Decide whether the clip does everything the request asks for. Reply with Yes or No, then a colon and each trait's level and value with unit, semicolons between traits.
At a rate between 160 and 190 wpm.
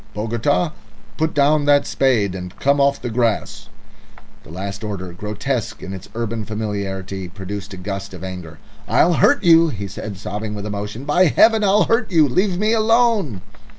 Yes: average, 170 wpm